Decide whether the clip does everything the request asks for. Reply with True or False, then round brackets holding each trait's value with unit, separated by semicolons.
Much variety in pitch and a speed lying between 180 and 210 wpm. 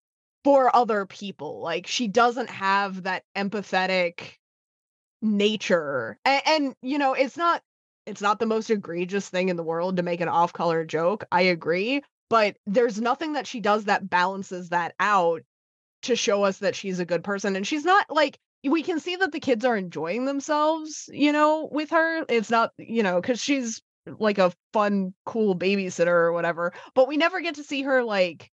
True (6.7 semitones; 185 wpm)